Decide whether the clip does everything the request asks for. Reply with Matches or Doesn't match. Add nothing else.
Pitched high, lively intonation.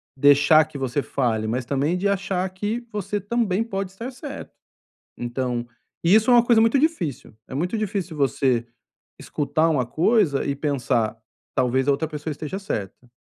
Doesn't match